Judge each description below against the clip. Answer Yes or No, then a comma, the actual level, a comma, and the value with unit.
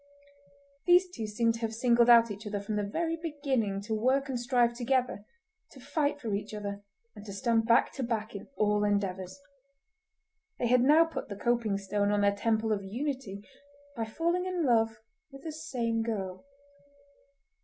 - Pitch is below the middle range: No, high, 230 Hz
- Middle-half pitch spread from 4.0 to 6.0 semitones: Yes, average, 4.3 semitones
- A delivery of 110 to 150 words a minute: No, average, 175 wpm